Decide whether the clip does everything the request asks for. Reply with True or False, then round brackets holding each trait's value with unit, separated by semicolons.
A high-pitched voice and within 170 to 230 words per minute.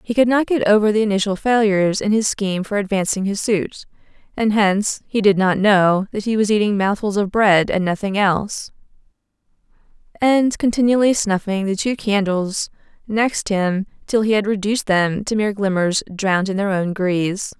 True (205 Hz; 175 wpm)